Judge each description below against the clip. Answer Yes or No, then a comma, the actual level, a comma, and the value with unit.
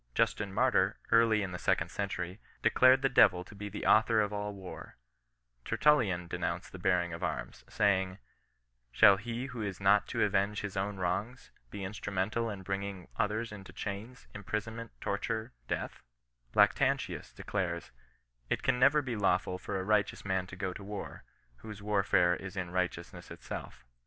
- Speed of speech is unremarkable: Yes, average, 170 wpm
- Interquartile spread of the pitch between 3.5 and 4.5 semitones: No, narrow, 2.6 semitones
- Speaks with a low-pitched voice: Yes, low, 100 Hz